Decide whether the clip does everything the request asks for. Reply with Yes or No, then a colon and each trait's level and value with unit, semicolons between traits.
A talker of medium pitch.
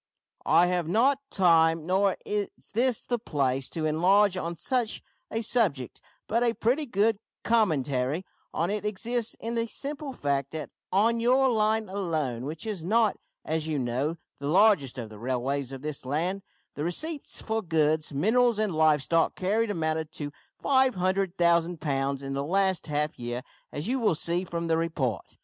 Yes: medium, 175 Hz